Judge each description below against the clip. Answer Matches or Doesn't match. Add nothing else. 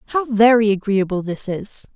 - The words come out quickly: Doesn't match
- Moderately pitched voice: Doesn't match